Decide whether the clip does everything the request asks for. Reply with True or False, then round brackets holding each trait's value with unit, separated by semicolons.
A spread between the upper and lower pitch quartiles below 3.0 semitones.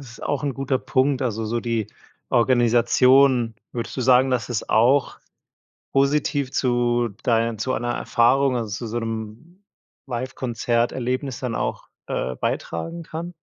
True (2.4 semitones)